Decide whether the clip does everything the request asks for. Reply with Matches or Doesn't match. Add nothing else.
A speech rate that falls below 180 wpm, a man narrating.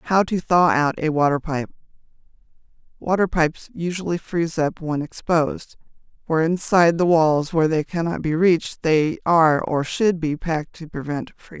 Doesn't match